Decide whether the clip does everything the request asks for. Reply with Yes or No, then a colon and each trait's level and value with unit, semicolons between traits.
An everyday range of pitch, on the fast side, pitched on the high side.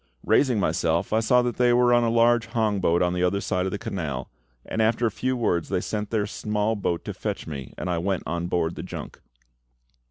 No: average, 4.9 semitones; fast, 230 wpm; low, 105 Hz